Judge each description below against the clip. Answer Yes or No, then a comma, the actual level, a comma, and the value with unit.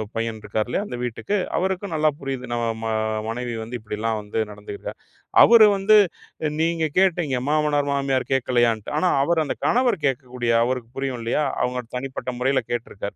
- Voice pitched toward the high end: No, low, 130 Hz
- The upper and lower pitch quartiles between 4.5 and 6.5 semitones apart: Yes, average, 5.0 semitones